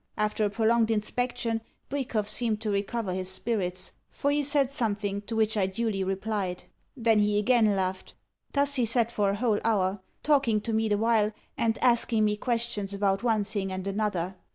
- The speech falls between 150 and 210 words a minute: Yes, average, 180 wpm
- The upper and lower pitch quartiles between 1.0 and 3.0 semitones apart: Yes, average, 2.7 semitones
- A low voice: No, high, 215 Hz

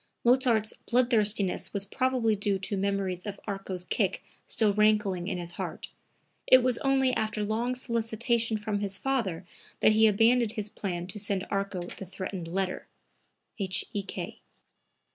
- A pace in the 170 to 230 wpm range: No, average, 145 wpm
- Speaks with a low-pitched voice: No, high, 210 Hz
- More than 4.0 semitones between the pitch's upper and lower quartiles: No, average, 3.0 semitones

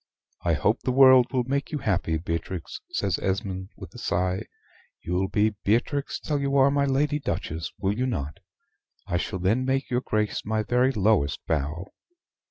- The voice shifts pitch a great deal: Yes, wide, 6.5 semitones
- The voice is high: No, low, 110 Hz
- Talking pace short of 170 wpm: No, average, 175 wpm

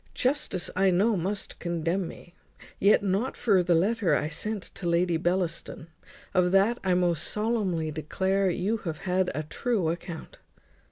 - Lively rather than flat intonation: No, average, 2.9 semitones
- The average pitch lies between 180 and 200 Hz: Yes, medium, 185 Hz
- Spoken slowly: No, average, 155 wpm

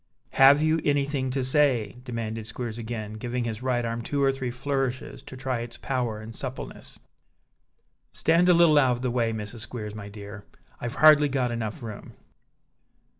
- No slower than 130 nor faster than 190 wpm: Yes, average, 175 wpm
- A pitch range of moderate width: Yes, average, 3.3 semitones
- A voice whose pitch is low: Yes, low, 125 Hz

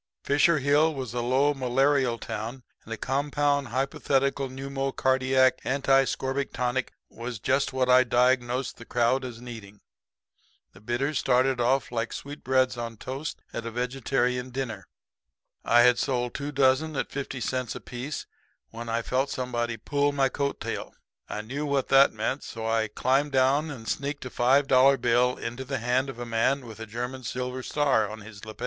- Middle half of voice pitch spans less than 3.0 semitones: Yes, narrow, 2.4 semitones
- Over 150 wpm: Yes, average, 170 wpm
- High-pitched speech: No, low, 130 Hz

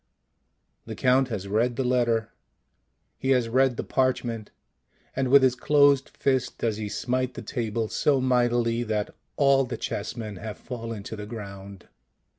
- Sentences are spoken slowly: No, average, 155 wpm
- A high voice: No, low, 120 Hz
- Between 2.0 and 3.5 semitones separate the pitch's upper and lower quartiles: Yes, average, 2.9 semitones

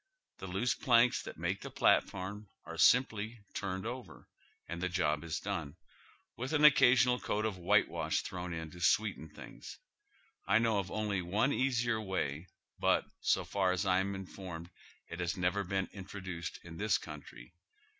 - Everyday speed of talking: Yes, average, 165 wpm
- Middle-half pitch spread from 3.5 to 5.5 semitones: Yes, average, 3.9 semitones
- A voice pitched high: No, very low, 95 Hz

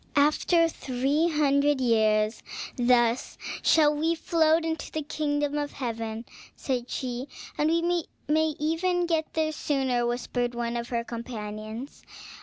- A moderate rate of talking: No, slow, 130 wpm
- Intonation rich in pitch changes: No, average, 4.6 semitones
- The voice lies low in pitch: No, very high, 280 Hz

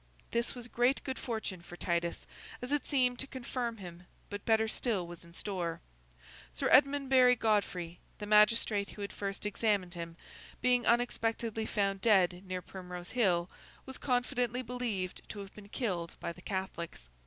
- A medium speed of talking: Yes, average, 160 wpm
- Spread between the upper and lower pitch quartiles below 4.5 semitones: No, average, 5.3 semitones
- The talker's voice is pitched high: Yes, high, 210 Hz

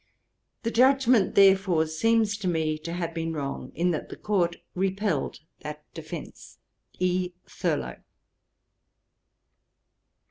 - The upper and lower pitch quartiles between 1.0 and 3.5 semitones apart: No, average, 3.9 semitones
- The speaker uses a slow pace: Yes, slow, 110 wpm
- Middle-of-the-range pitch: Yes, medium, 180 Hz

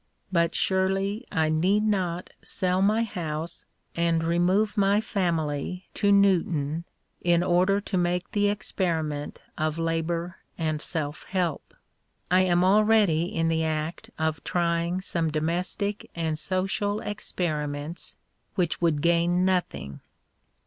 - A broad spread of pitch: No, average, 3.0 semitones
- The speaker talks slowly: Yes, slow, 120 wpm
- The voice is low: No, medium, 175 Hz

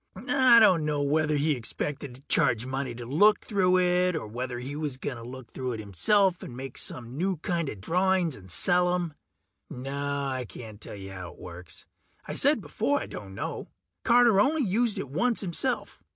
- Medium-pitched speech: Yes, medium, 145 Hz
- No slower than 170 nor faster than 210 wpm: Yes, average, 185 wpm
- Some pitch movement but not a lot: No, wide, 6.8 semitones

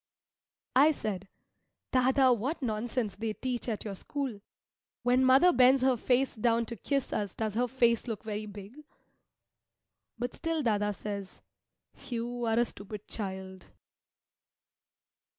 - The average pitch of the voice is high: Yes, high, 235 Hz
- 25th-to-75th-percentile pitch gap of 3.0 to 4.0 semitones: Yes, average, 3.5 semitones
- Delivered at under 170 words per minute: Yes, slow, 135 wpm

